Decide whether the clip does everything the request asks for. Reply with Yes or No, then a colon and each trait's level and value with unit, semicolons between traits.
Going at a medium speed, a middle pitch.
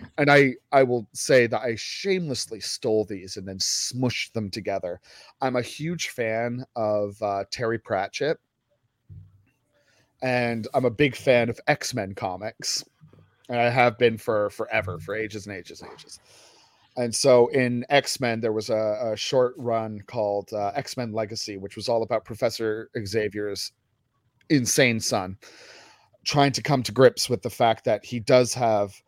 No: average, 165 wpm; low, 115 Hz